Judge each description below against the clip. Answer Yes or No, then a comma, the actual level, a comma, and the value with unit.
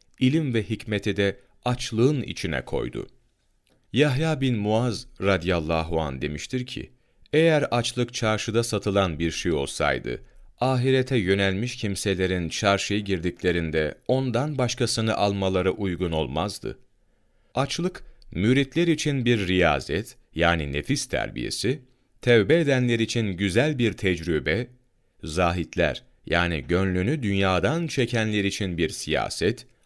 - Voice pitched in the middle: No, low, 105 Hz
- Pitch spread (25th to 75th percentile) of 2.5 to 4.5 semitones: No, average, 5.3 semitones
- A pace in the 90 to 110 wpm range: Yes, average, 105 wpm